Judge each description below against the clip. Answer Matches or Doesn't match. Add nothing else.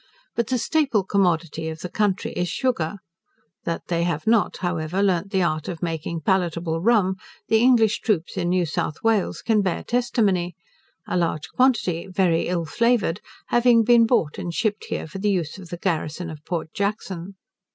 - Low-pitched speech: Doesn't match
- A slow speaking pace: Doesn't match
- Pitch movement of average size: Matches